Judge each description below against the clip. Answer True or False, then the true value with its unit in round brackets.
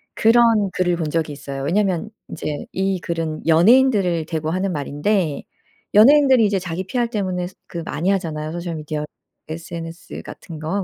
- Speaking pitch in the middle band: True (175 Hz)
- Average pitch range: True (4.0 semitones)